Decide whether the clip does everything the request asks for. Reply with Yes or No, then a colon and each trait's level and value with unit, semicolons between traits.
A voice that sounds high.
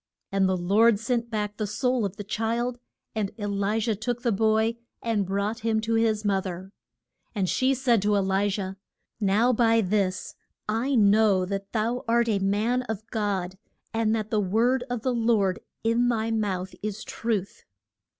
Yes: high, 215 Hz